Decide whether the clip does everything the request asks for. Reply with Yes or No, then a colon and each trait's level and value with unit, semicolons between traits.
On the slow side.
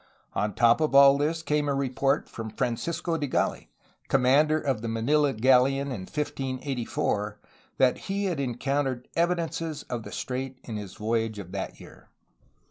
No: average, 155 wpm